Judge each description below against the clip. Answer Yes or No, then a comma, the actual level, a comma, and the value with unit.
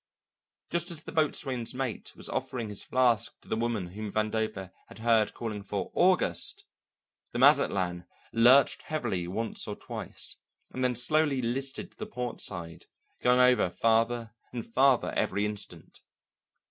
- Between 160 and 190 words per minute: No, average, 145 wpm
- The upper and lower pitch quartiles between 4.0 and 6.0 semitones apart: No, average, 3.5 semitones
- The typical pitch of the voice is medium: No, low, 115 Hz